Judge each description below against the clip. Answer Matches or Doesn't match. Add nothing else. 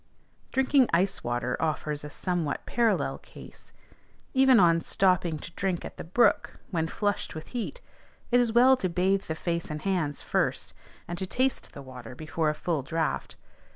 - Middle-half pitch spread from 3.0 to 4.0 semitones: Doesn't match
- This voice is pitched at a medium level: Matches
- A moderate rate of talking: Matches